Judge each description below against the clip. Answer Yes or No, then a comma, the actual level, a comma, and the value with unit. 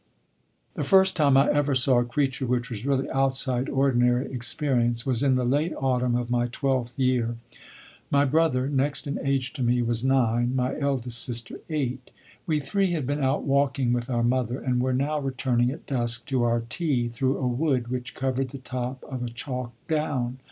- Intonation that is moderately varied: No, narrow, 2.2 semitones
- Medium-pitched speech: No, low, 130 Hz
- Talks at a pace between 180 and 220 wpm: Yes, average, 190 wpm